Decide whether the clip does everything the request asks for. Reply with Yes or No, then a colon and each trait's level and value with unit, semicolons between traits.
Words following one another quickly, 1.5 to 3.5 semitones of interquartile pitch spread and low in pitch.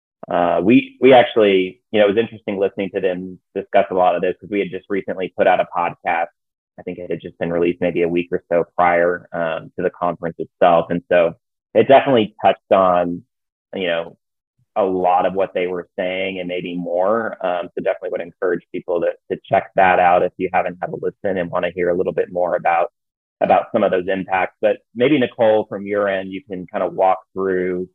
Yes: fast, 225 wpm; average, 3.1 semitones; very low, 95 Hz